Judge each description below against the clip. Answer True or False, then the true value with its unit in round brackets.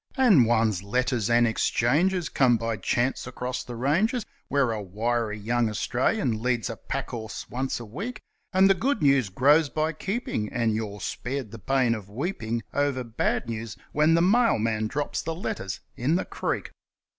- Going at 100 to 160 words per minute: False (170 wpm)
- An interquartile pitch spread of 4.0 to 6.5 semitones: True (5.3 semitones)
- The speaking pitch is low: True (125 Hz)